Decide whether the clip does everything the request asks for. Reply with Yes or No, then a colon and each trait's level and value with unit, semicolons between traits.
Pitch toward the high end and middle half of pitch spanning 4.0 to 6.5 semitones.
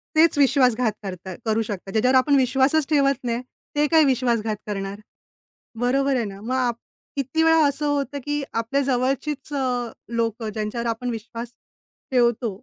No: very high, 250 Hz; average, 3.5 semitones